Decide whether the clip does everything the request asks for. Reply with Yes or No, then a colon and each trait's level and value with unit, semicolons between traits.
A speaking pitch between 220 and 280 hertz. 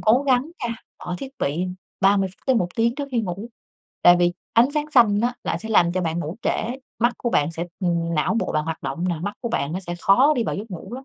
No: high, 205 Hz